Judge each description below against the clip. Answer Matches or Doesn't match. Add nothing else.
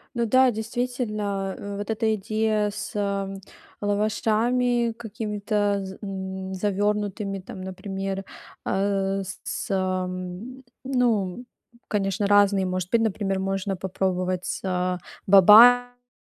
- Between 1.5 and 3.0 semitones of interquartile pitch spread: Matches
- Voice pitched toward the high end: Matches